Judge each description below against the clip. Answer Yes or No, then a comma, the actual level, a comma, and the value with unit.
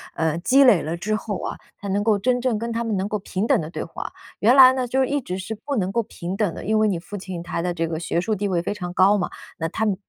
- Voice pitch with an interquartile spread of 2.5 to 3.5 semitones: No, average, 4.3 semitones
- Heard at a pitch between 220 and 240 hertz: No, high, 205 Hz